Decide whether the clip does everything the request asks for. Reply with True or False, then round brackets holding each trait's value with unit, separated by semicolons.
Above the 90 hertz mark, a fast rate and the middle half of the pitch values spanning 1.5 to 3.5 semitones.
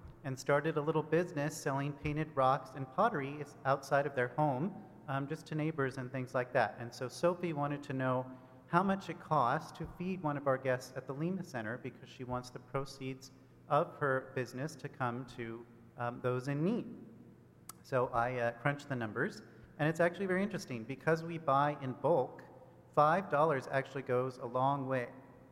False (135 Hz; 185 wpm; 3.2 semitones)